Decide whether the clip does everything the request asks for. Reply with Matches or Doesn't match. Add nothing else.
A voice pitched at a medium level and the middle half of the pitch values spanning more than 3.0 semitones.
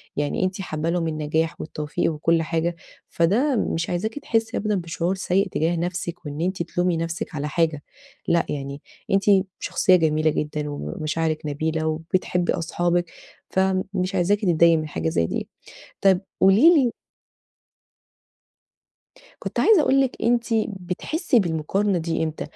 Matches